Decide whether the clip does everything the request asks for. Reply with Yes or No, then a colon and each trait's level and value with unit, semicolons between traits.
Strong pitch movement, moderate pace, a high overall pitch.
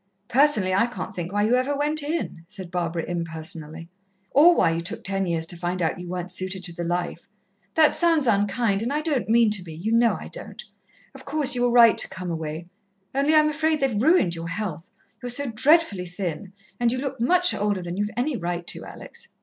No: wide, 7.5 semitones; fast, 215 wpm; high, 205 Hz